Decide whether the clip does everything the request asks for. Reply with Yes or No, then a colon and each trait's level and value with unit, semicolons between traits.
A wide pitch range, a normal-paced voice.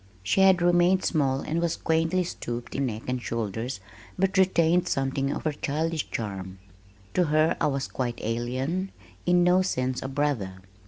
Yes: wide, 6.1 semitones; average, 165 wpm